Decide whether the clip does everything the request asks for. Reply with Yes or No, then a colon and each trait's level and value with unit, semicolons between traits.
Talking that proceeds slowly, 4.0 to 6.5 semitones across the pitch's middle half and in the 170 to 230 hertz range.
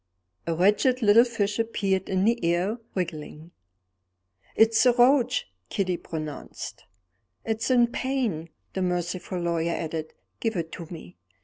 Yes: slow, 130 wpm; average, 5.3 semitones; high, 190 Hz